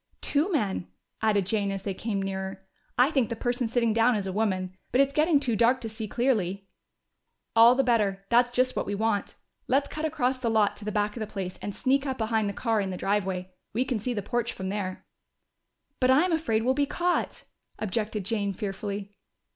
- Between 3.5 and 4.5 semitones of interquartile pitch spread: Yes, average, 4.0 semitones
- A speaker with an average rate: No, fast, 210 wpm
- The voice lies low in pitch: No, high, 220 Hz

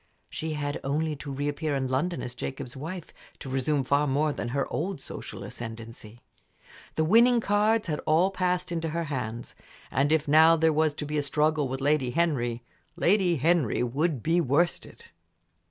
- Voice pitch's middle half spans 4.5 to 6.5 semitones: No, average, 3.9 semitones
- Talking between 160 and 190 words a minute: Yes, average, 170 wpm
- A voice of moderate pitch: Yes, medium, 150 Hz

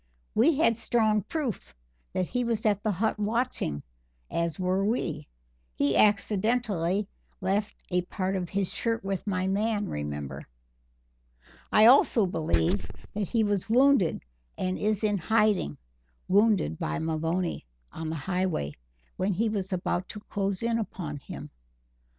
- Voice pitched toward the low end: No, high, 195 Hz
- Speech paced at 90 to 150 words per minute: Yes, average, 140 wpm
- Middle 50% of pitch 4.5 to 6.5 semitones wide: No, average, 3.8 semitones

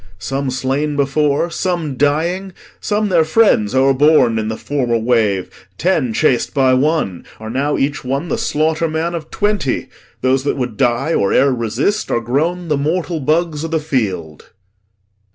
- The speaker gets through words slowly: No, average, 160 wpm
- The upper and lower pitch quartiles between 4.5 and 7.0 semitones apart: Yes, average, 5.1 semitones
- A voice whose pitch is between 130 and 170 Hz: Yes, medium, 140 Hz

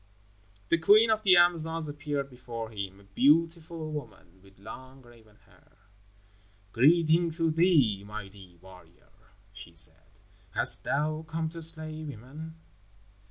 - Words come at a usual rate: No, slow, 125 wpm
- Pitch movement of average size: No, wide, 8.1 semitones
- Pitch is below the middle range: No, medium, 145 Hz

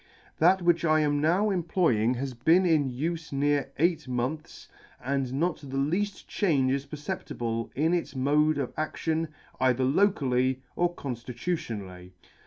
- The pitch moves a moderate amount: Yes, average, 4.4 semitones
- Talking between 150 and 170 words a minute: No, average, 140 wpm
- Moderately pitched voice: Yes, medium, 145 Hz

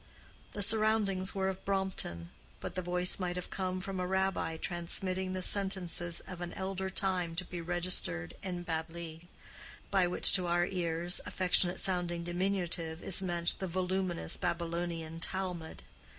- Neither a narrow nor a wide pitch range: No, narrow, 1.8 semitones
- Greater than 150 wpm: No, average, 145 wpm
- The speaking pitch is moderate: Yes, medium, 180 Hz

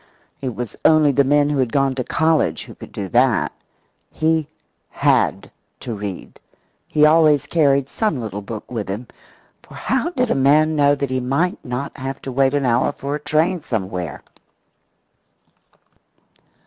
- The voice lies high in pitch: No, medium, 140 Hz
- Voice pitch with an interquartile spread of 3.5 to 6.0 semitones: Yes, average, 3.8 semitones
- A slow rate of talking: No, average, 160 wpm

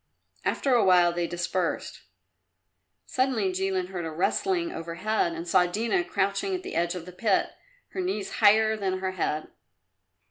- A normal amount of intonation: Yes, average, 4.0 semitones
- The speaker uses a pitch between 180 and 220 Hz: Yes, high, 190 Hz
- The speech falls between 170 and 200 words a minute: No, average, 155 wpm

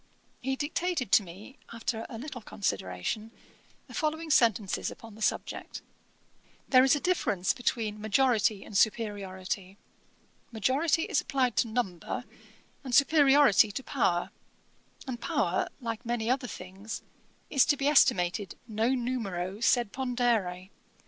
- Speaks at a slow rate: Yes, slow, 130 wpm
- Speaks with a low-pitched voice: No, high, 230 Hz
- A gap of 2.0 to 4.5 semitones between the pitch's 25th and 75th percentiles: No, average, 4.9 semitones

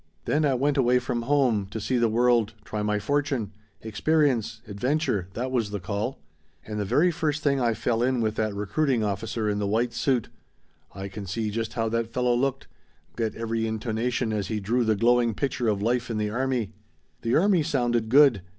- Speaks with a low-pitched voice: Yes, low, 115 Hz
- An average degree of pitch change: Yes, average, 3.2 semitones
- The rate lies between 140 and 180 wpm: No, average, 195 wpm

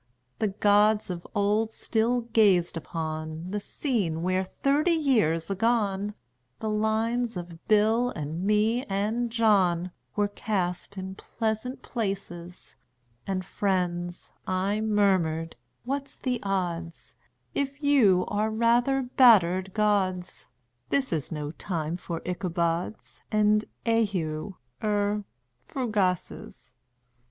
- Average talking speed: No, slow, 110 wpm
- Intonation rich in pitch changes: No, average, 4.0 semitones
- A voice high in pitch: Yes, high, 205 Hz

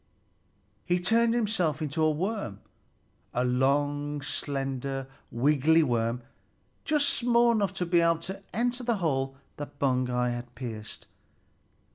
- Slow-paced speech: Yes, slow, 125 wpm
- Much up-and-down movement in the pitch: Yes, wide, 6.7 semitones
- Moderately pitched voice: Yes, medium, 145 Hz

